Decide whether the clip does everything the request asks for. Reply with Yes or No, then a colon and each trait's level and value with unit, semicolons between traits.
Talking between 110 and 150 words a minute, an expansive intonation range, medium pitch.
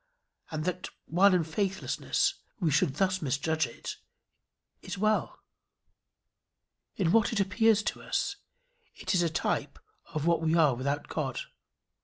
No: average, 140 wpm; average, 4.2 semitones; medium, 170 Hz